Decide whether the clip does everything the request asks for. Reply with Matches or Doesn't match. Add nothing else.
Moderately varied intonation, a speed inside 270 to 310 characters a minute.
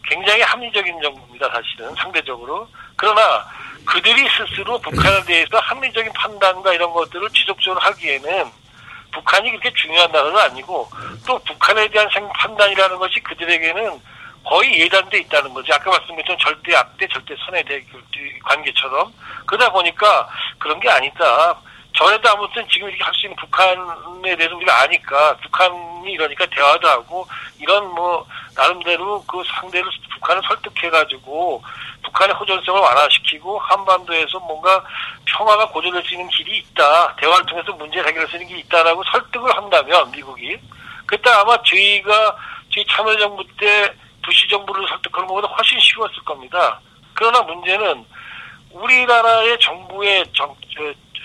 Doesn't match